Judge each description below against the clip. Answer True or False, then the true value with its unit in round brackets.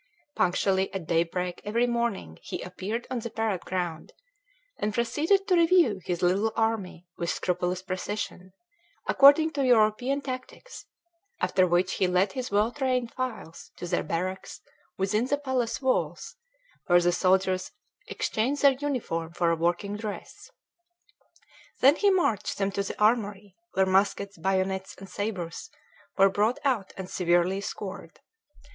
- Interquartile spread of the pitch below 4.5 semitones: False (5.0 semitones)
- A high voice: True (200 Hz)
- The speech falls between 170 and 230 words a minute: False (140 wpm)